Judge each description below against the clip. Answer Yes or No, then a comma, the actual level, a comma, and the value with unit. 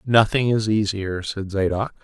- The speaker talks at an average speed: Yes, average, 150 wpm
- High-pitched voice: No, low, 105 Hz